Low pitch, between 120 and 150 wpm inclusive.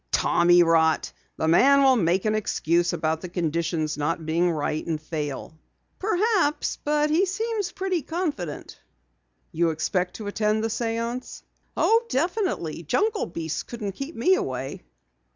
No: high, 190 Hz; slow, 135 wpm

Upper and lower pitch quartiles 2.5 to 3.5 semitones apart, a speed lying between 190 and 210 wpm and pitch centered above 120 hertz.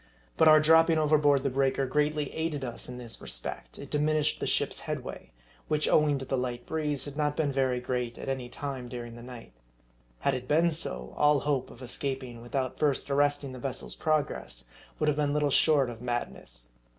Yes: average, 3.2 semitones; average, 200 wpm; medium, 140 Hz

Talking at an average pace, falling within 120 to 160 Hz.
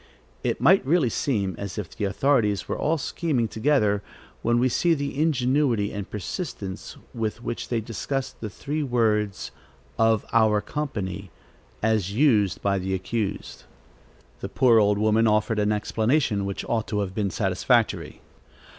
No: average, 150 wpm; low, 110 Hz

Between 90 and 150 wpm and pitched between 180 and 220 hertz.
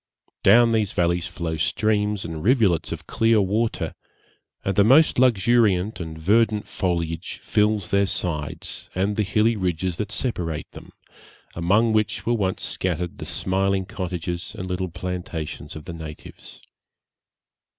No: average, 140 wpm; very low, 95 Hz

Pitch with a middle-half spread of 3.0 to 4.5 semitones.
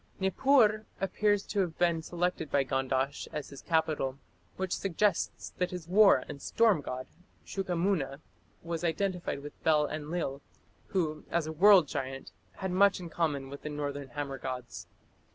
No: average, 5.0 semitones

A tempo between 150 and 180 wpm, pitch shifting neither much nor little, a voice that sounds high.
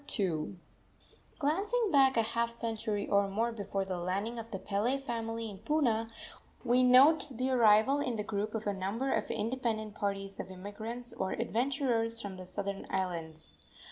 Yes: average, 165 wpm; average, 3.7 semitones; high, 225 Hz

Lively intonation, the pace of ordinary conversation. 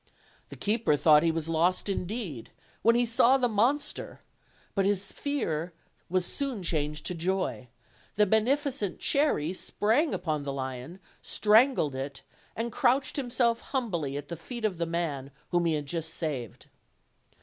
Yes: wide, 7.3 semitones; average, 150 wpm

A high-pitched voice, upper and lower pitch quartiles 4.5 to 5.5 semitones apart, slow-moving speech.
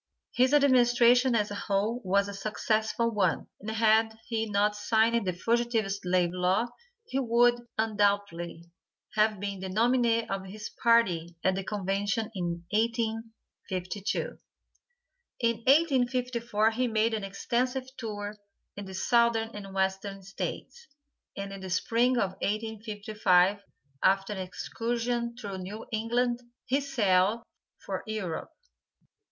No: high, 215 Hz; average, 3.1 semitones; slow, 125 wpm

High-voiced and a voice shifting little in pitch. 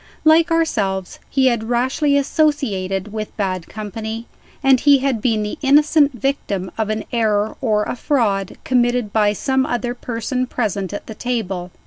No: high, 230 Hz; average, 4.3 semitones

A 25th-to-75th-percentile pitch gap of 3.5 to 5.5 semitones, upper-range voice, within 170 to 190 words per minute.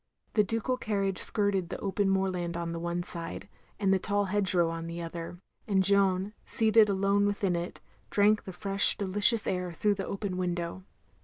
No: narrow, 2.5 semitones; high, 195 Hz; average, 180 wpm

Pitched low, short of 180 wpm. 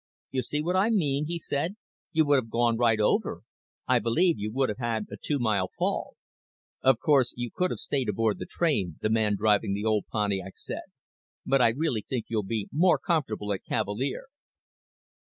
No: low, 120 Hz; average, 190 wpm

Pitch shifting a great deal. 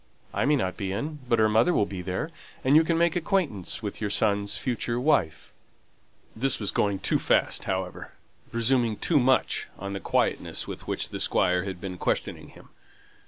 Yes: wide, 5.7 semitones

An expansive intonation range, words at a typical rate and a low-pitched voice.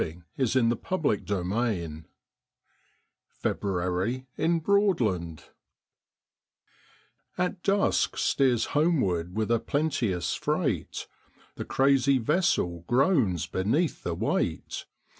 No: wide, 8.7 semitones; slow, 105 wpm; low, 120 Hz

